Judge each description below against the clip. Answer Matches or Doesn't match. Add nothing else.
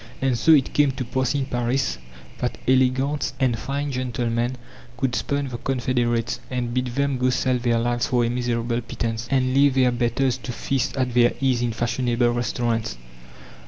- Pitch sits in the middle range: Doesn't match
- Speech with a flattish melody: Matches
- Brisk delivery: Doesn't match